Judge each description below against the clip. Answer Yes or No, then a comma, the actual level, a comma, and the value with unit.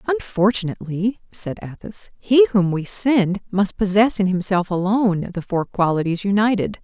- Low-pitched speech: No, high, 200 Hz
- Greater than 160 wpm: No, average, 140 wpm